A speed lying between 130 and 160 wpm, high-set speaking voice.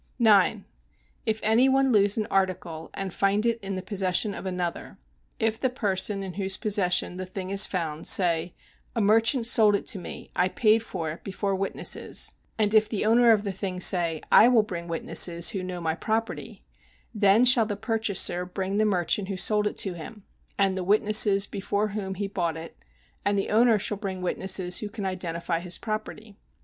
No: average, 190 wpm; high, 195 Hz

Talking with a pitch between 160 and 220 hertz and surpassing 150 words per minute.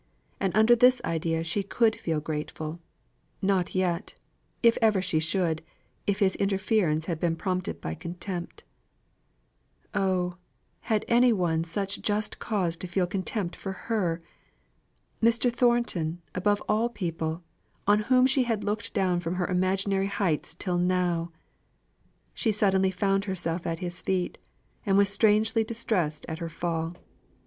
No: high, 190 Hz; average, 140 wpm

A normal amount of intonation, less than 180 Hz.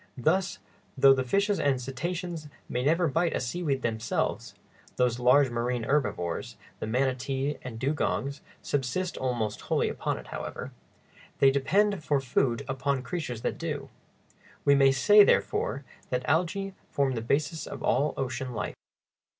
Yes: average, 3.9 semitones; low, 135 Hz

